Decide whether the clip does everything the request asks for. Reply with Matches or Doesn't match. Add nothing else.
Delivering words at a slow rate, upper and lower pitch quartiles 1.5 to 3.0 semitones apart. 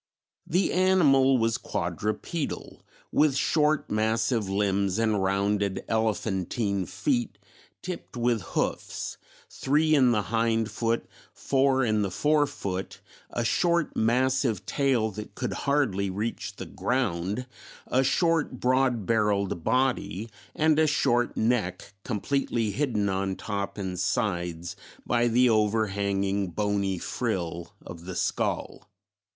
Doesn't match